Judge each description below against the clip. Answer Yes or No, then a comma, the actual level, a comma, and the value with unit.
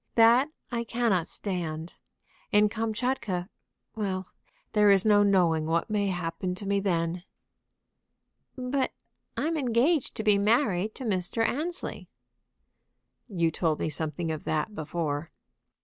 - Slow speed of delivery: Yes, slow, 125 wpm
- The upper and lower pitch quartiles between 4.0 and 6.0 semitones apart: Yes, average, 5.1 semitones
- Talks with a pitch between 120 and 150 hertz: No, high, 200 Hz